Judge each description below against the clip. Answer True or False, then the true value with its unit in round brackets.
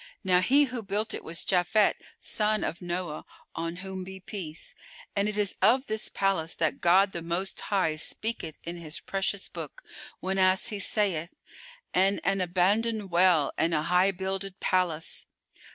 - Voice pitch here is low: False (190 Hz)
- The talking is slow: False (160 wpm)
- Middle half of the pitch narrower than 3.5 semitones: True (2.8 semitones)